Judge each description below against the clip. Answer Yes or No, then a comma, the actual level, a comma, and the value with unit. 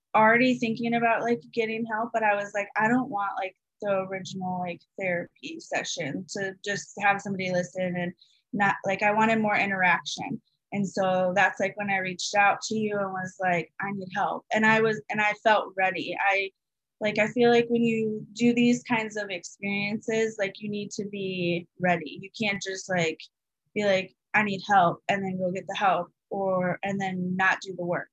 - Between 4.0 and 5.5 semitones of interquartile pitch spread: No, average, 2.7 semitones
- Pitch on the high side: Yes, high, 200 Hz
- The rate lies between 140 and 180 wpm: No, average, 200 wpm